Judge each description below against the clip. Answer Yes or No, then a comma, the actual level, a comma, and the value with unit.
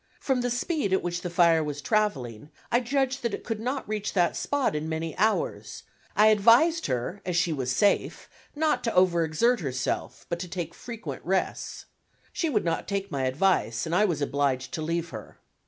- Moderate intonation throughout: No, wide, 6.5 semitones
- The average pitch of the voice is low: No, medium, 180 Hz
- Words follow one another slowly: No, average, 195 wpm